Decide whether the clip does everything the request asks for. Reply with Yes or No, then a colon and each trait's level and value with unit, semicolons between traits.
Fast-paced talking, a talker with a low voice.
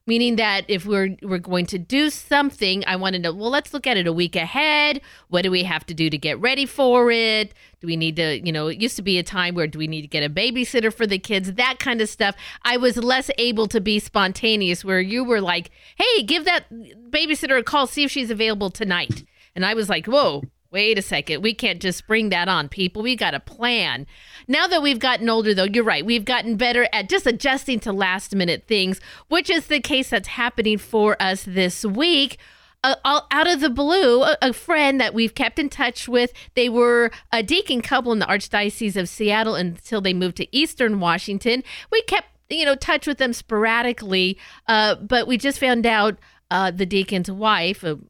No: fast, 220 wpm; high, 225 Hz